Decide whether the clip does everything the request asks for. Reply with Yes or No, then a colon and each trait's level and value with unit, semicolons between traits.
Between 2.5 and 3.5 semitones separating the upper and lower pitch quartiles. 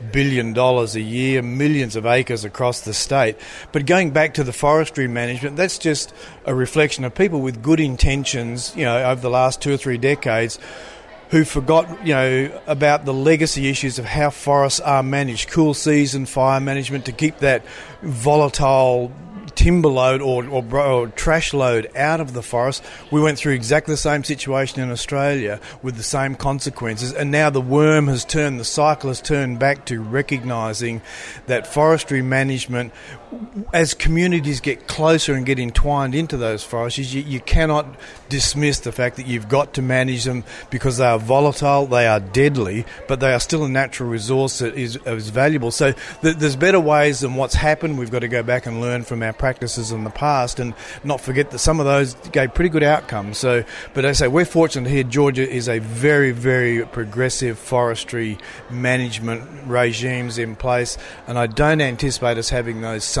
Yes: average, 3.2 semitones